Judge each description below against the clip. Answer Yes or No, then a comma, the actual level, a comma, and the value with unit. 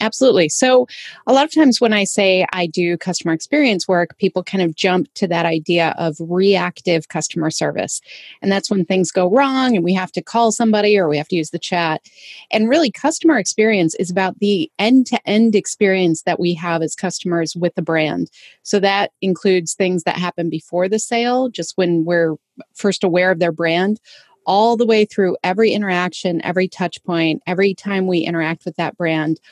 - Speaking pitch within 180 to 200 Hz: Yes, medium, 185 Hz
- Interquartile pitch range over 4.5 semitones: No, average, 3.6 semitones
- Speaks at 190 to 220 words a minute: Yes, average, 195 wpm